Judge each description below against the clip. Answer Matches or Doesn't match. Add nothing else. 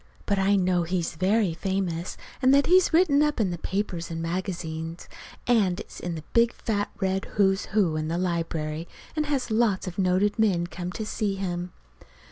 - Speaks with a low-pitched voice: Doesn't match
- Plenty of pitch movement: Doesn't match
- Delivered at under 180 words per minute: Doesn't match